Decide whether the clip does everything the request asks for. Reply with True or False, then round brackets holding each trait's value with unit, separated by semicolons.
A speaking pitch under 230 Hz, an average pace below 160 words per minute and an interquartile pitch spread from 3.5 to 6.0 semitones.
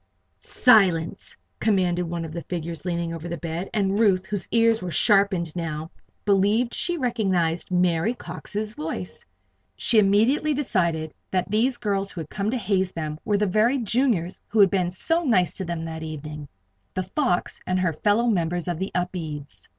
False (185 Hz; 175 wpm; 4.2 semitones)